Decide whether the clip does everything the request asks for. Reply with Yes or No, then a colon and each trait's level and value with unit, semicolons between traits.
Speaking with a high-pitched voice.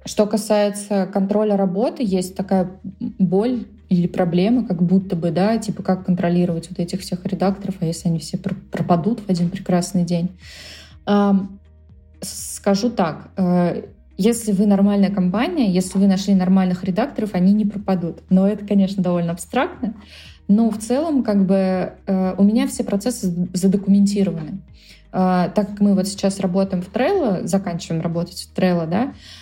Yes: high, 195 Hz